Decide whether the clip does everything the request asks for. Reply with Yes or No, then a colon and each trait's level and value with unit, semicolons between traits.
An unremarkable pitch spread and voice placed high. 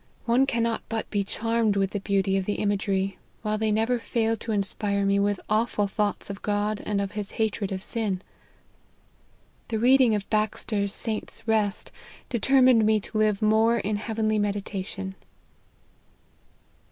No: narrow, 1.9 semitones; high, 210 Hz